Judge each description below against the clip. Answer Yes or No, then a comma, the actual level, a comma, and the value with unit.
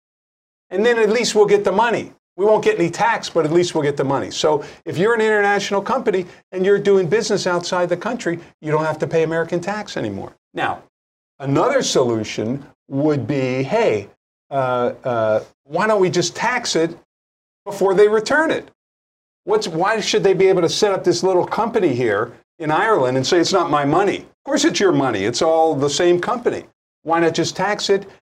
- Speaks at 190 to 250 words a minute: Yes, average, 200 wpm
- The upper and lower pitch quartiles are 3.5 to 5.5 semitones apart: Yes, average, 4.5 semitones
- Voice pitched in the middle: Yes, medium, 180 Hz